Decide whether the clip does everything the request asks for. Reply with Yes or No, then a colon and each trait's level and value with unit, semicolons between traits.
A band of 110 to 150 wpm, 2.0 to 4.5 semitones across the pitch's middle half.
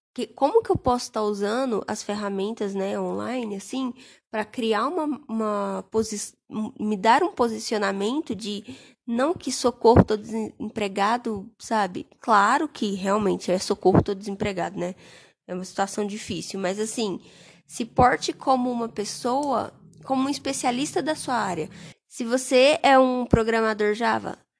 Yes: average, 140 wpm; average, 3.9 semitones